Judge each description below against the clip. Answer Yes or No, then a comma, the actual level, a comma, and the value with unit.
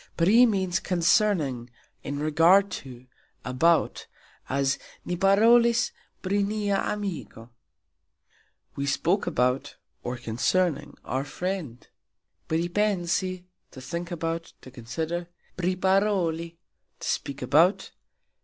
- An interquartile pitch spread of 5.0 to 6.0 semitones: Yes, wide, 5.6 semitones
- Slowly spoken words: Yes, slow, 100 wpm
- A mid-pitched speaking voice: Yes, medium, 170 Hz